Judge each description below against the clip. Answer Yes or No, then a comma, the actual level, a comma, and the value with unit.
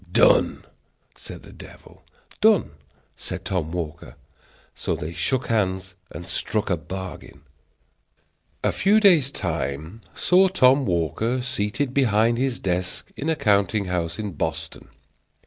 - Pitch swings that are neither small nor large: No, wide, 7.0 semitones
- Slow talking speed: Yes, slow, 130 wpm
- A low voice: Yes, low, 105 Hz